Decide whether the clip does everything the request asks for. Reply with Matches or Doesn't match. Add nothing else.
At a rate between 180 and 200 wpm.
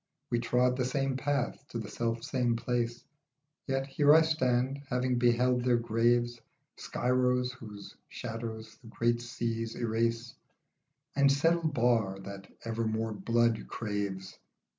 Doesn't match